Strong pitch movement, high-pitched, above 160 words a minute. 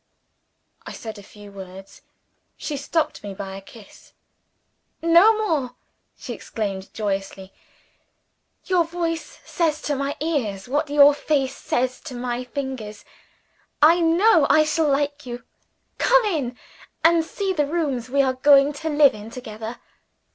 No: wide, 6.1 semitones; very high, 280 Hz; average, 140 wpm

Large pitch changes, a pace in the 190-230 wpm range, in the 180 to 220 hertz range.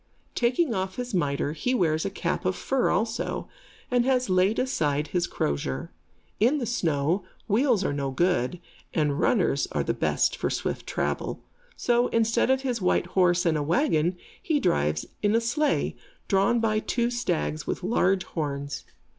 No: wide, 7.3 semitones; average, 165 wpm; high, 190 Hz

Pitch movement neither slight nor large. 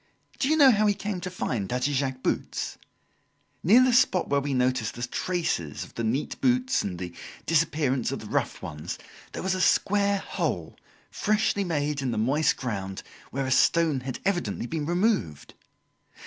No: wide, 8.0 semitones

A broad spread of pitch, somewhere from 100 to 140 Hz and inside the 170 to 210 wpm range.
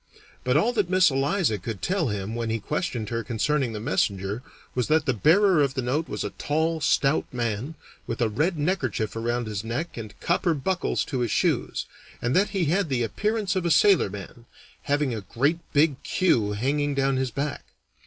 Yes: wide, 6.1 semitones; low, 135 Hz; average, 195 wpm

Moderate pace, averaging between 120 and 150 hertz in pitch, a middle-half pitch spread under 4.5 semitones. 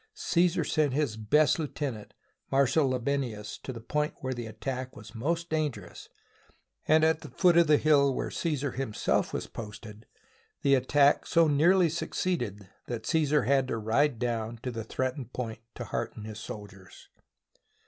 No: average, 160 wpm; low, 135 Hz; average, 5.2 semitones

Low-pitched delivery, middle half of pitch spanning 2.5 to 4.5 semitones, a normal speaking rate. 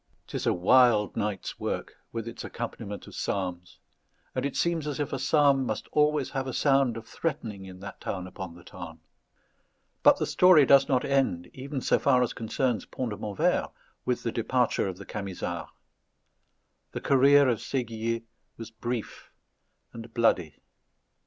No: low, 115 Hz; average, 4.9 semitones; average, 165 wpm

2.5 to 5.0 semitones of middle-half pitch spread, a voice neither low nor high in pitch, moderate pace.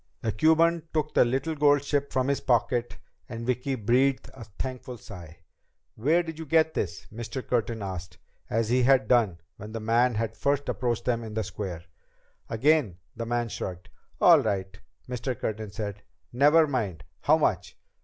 No: average, 4.2 semitones; low, 120 Hz; average, 170 wpm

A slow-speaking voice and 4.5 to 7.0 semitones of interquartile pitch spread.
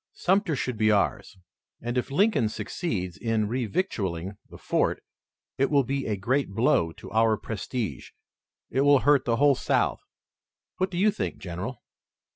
No: average, 155 wpm; wide, 5.4 semitones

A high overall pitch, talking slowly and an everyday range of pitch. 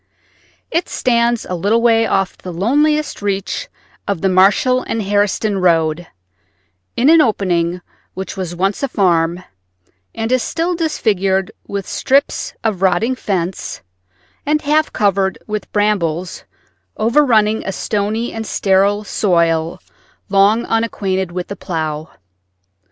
Yes: high, 200 Hz; slow, 125 wpm; average, 4.0 semitones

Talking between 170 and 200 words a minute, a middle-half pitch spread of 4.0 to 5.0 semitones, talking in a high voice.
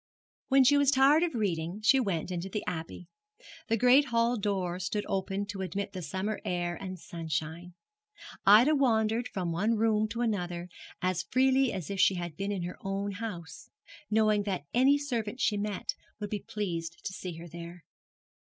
Yes: average, 180 wpm; average, 4.3 semitones; high, 200 Hz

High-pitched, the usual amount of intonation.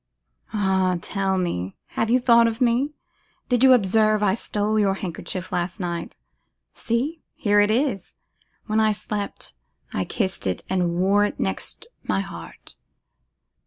Yes: high, 205 Hz; average, 3.7 semitones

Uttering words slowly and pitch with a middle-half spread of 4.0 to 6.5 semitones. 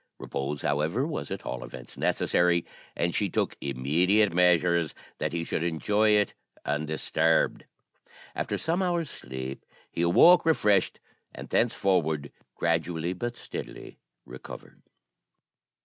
Yes: slow, 115 wpm; average, 5.2 semitones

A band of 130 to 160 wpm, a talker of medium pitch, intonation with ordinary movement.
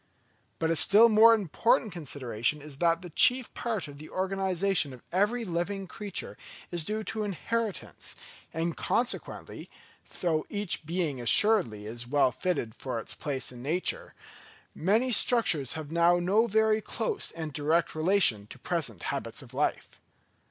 No: average, 150 wpm; medium, 175 Hz; wide, 6.2 semitones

